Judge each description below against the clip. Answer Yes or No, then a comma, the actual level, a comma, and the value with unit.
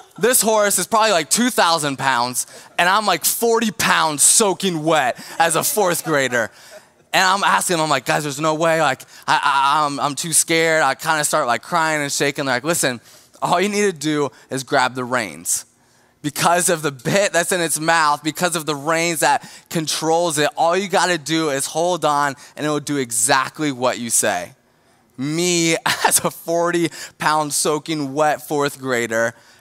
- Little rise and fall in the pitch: No, average, 3.3 semitones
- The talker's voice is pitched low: No, medium, 155 Hz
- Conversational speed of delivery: Yes, average, 195 wpm